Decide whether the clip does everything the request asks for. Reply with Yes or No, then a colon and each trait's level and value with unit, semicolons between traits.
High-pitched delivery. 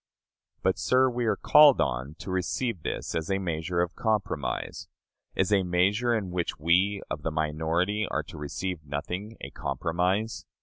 No: very low, 90 Hz